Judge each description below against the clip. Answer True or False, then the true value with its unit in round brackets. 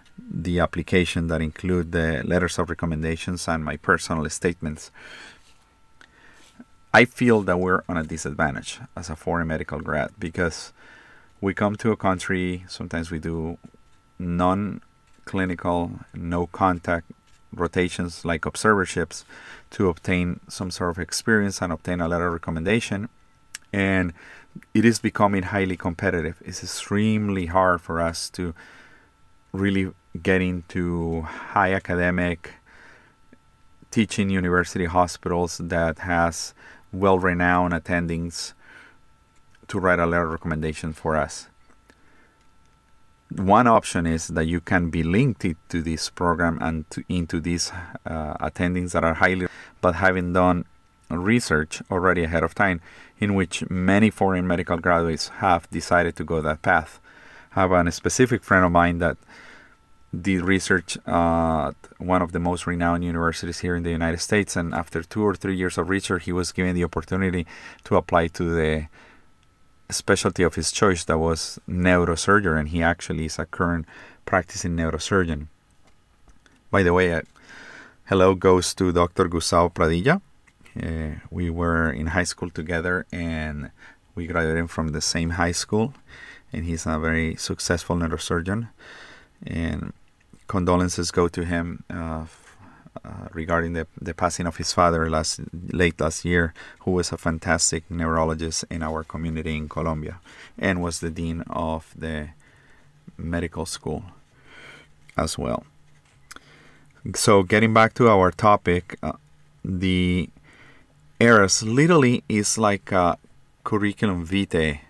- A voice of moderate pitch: False (85 Hz)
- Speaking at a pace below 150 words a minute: True (135 wpm)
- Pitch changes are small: True (2.3 semitones)